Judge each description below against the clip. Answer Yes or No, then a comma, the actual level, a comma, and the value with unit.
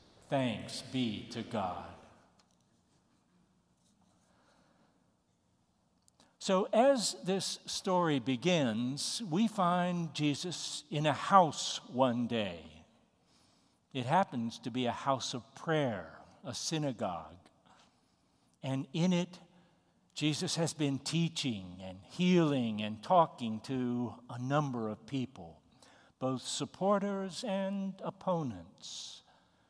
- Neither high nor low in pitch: Yes, medium, 145 Hz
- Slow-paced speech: Yes, slow, 95 wpm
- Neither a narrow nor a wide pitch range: No, wide, 6.8 semitones